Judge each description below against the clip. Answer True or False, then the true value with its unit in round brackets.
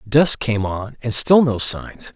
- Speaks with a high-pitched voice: False (120 Hz)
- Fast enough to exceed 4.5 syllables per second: False (3.5 syllables/s)